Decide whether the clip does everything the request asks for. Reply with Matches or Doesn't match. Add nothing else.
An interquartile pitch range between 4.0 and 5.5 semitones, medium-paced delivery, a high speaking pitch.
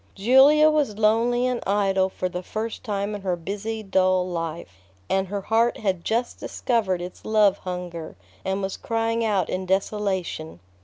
Doesn't match